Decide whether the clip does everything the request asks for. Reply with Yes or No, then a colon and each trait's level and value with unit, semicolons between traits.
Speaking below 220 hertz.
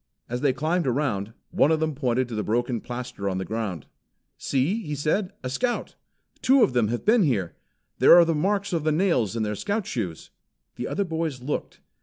Yes: low, 135 Hz